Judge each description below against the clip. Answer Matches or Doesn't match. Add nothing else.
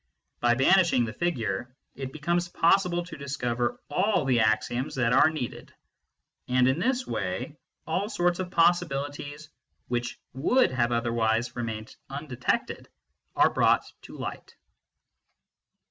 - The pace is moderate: Doesn't match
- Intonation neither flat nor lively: Doesn't match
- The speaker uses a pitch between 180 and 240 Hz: Doesn't match